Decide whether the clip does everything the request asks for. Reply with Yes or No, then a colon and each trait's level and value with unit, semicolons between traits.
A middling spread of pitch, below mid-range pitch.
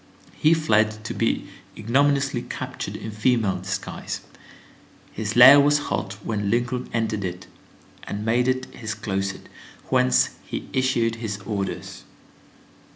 Yes: average, 3.9 semitones; low, 110 Hz